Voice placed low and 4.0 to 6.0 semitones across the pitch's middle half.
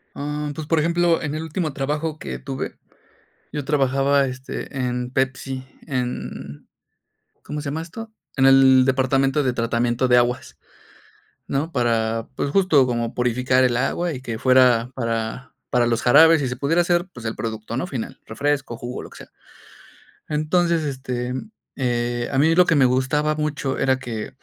No: low, 130 Hz; average, 3.5 semitones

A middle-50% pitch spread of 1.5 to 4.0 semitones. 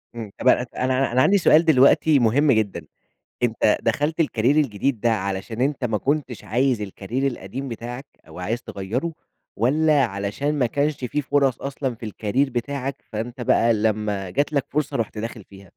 No: average, 4.4 semitones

